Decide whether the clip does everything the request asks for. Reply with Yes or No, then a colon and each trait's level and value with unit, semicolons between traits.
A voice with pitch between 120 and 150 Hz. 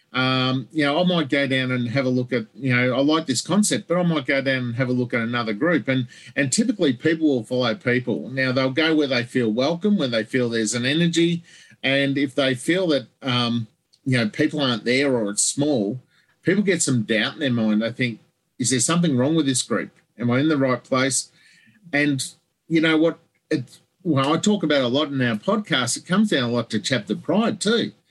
Yes: low, 135 Hz